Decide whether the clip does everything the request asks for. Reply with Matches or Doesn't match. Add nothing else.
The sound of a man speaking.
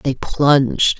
Doesn't match